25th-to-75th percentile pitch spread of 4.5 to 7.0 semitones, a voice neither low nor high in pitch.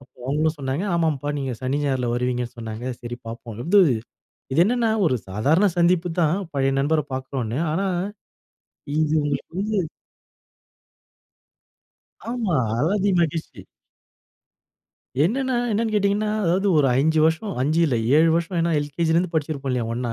Yes: average, 5.2 semitones; medium, 155 Hz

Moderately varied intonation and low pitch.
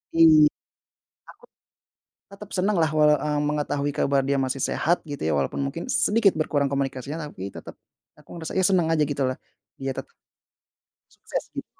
No: average, 3.1 semitones; medium, 150 Hz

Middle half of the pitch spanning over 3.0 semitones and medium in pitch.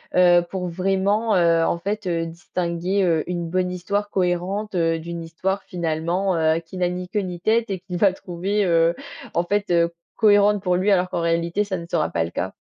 No: narrow, 2.5 semitones; medium, 180 Hz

